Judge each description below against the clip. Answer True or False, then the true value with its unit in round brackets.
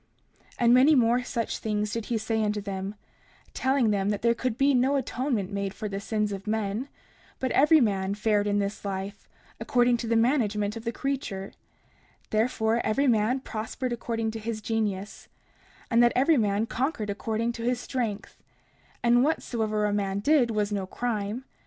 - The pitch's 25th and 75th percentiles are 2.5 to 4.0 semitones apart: True (2.9 semitones)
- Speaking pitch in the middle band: False (225 Hz)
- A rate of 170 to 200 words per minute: True (175 wpm)